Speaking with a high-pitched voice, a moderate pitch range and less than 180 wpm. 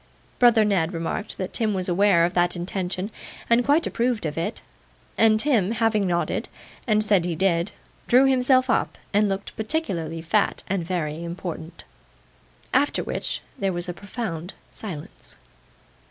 Yes: high, 195 Hz; average, 4.2 semitones; average, 150 wpm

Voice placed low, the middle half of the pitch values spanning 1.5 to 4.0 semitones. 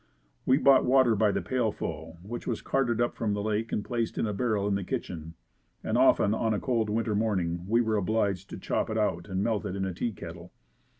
Yes: low, 105 Hz; average, 3.1 semitones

